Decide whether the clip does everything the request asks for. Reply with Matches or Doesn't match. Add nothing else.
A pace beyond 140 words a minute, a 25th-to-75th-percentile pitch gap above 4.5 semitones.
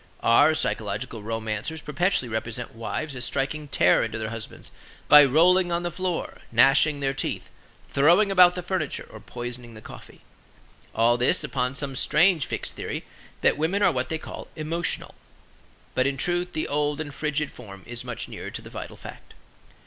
Matches